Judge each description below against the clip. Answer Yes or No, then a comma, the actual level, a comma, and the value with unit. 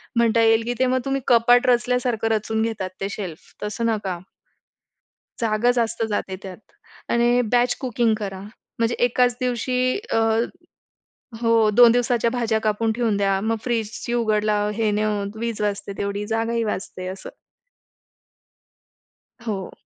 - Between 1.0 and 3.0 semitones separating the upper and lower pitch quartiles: Yes, narrow, 2.4 semitones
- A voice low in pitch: No, high, 225 Hz